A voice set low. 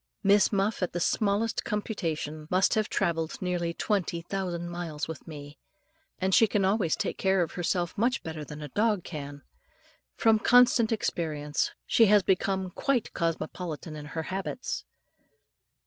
No: medium, 180 Hz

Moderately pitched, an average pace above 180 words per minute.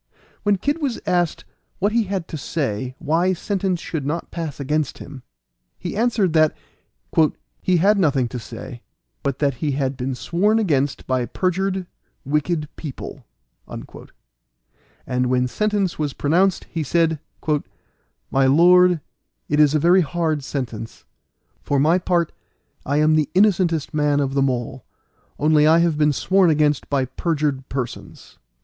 No: medium, 155 Hz; average, 145 wpm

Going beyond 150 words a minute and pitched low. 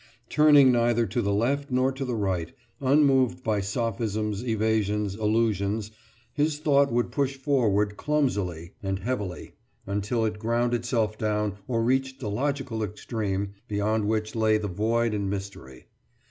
No: average, 145 wpm; low, 110 Hz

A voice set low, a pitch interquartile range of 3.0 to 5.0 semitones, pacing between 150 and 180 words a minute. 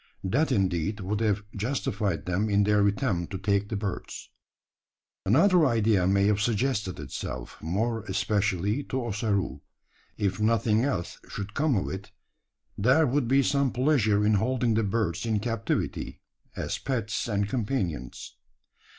No: low, 105 Hz; average, 3.4 semitones; average, 140 wpm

